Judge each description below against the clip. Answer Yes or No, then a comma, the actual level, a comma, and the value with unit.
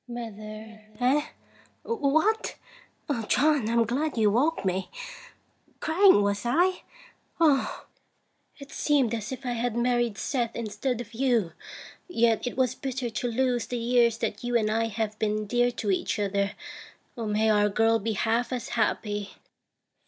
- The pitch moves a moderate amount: Yes, average, 3.1 semitones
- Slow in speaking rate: No, average, 145 wpm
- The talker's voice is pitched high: Yes, high, 235 Hz